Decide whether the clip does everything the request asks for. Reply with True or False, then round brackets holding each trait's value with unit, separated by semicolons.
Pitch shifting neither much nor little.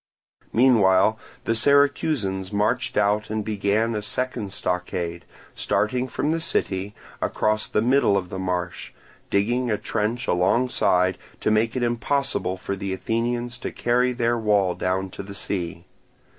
True (4.0 semitones)